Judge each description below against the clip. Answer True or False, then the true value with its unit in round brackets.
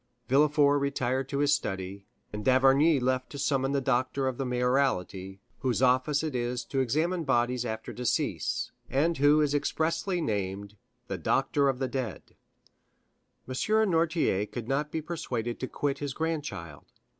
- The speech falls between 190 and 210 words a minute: False (155 wpm)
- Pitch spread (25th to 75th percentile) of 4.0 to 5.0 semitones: False (3.3 semitones)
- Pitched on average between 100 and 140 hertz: True (135 Hz)